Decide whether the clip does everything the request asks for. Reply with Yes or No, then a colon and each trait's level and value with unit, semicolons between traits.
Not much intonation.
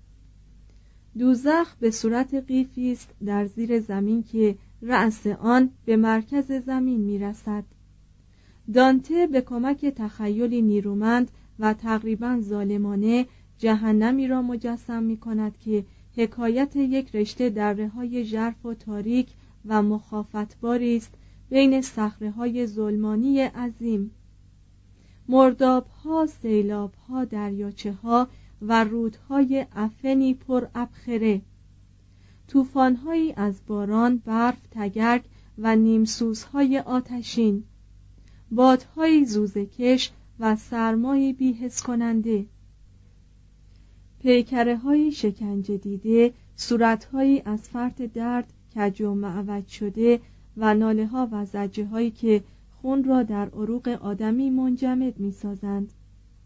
No: average, 3.4 semitones